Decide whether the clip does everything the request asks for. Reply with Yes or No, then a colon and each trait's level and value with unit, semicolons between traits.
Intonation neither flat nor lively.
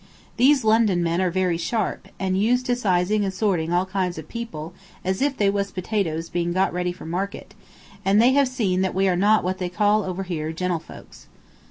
Yes: average, 3.3 semitones